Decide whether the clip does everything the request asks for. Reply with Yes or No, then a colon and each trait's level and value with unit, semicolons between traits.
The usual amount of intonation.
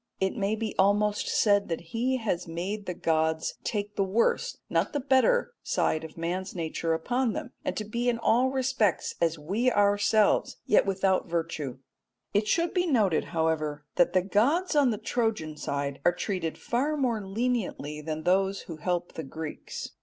No: wide, 6.1 semitones